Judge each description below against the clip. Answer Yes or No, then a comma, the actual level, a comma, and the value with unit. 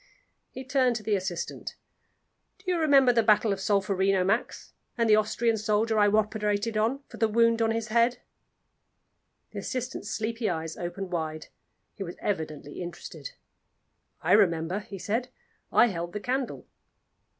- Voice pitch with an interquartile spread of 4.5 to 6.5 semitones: No, average, 3.4 semitones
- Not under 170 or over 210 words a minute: No, average, 150 wpm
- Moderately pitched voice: No, high, 215 Hz